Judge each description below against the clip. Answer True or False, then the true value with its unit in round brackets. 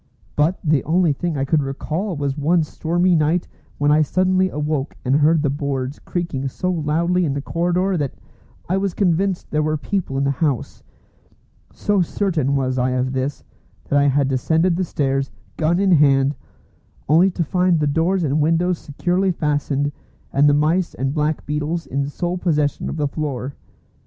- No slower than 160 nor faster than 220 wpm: True (175 wpm)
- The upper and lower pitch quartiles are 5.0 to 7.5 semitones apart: False (3.7 semitones)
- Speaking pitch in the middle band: True (155 Hz)